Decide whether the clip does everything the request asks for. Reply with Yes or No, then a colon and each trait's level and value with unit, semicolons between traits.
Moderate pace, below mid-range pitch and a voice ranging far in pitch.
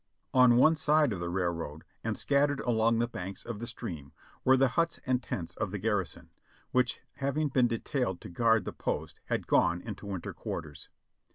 Yes: average, 185 wpm; low, 115 Hz; wide, 5.8 semitones